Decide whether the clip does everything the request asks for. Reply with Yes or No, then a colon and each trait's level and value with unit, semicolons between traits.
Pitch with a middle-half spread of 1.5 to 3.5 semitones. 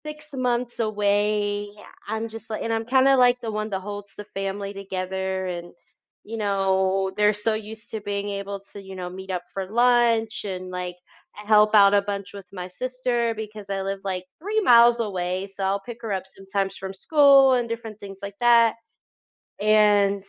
Yes: average, 2.8 semitones